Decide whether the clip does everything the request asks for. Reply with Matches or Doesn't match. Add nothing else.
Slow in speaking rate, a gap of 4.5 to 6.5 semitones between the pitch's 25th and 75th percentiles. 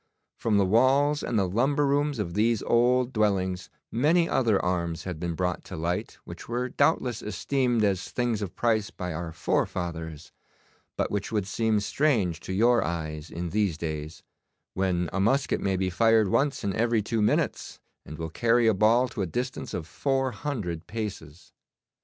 Doesn't match